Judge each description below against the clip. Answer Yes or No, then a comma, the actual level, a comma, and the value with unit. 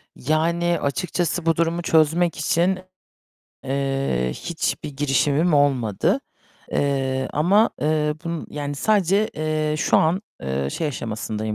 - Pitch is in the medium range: Yes, medium, 150 Hz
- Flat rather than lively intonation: No, average, 3.8 semitones